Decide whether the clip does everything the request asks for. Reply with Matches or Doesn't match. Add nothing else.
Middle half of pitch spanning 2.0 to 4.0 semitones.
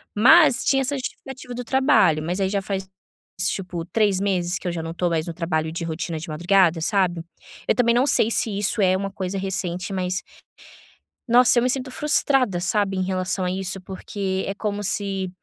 Matches